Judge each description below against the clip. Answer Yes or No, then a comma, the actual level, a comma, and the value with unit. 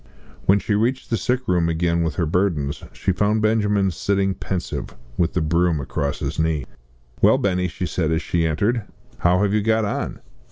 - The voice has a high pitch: No, very low, 90 Hz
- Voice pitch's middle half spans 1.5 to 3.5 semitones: No, average, 3.9 semitones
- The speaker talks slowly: No, average, 190 wpm